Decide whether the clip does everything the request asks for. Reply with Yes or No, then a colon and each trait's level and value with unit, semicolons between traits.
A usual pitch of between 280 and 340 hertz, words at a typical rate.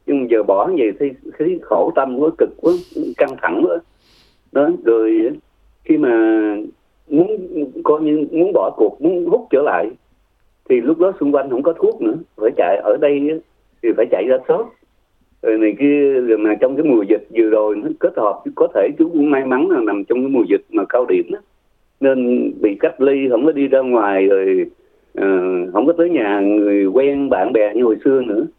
Yes: very high, 325 Hz; average, 210 wpm